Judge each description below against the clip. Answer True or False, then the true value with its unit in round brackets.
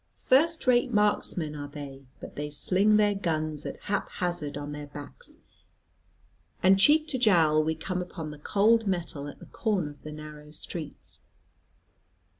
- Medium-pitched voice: True (165 Hz)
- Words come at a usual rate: True (160 wpm)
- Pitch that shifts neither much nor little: False (5.7 semitones)